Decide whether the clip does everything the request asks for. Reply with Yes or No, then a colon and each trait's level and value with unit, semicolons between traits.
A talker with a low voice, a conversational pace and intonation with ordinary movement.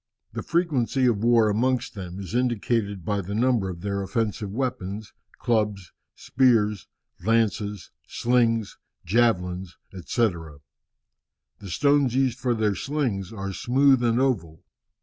No: low, 110 Hz; slow, 125 wpm; average, 4.0 semitones